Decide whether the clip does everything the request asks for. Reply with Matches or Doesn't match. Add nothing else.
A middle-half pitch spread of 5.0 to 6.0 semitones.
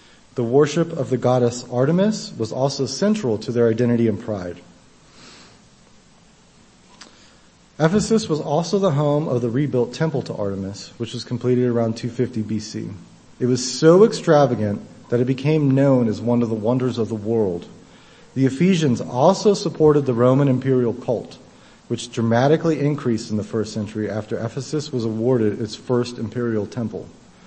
Doesn't match